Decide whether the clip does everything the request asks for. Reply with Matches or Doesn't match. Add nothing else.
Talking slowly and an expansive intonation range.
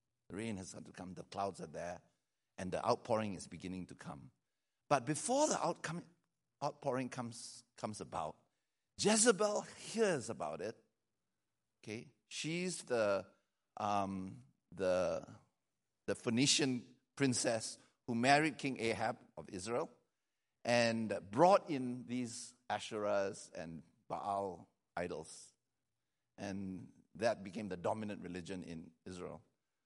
Matches